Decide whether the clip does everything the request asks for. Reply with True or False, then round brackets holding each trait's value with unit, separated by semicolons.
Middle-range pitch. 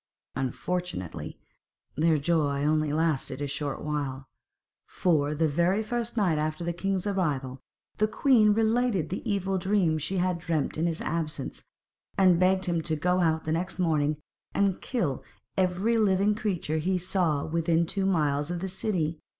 True (170 Hz)